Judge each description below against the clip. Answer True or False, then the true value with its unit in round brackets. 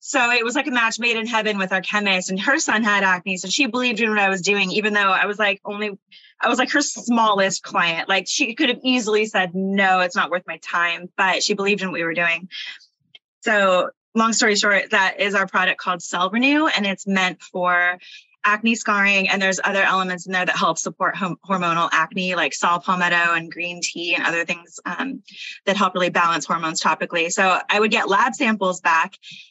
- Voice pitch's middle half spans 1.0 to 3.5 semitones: True (3.2 semitones)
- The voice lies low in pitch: False (195 Hz)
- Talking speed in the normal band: False (220 wpm)